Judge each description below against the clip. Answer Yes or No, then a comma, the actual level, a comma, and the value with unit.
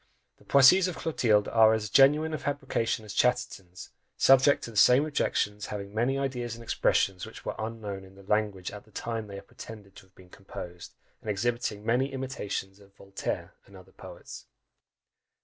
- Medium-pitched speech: No, low, 110 Hz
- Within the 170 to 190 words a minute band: Yes, average, 180 wpm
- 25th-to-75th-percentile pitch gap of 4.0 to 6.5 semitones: Yes, average, 4.4 semitones